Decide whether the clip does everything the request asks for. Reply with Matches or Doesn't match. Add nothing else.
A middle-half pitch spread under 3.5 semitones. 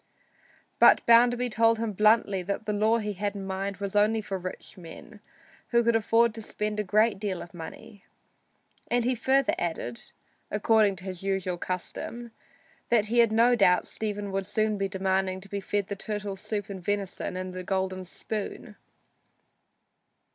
Matches